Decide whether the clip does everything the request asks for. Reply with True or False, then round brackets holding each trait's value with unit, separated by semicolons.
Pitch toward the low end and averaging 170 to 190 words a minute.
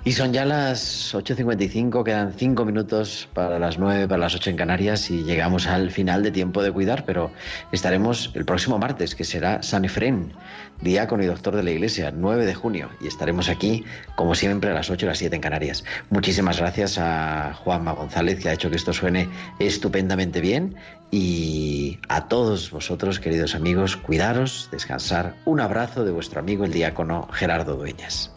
True (95 Hz; 180 wpm)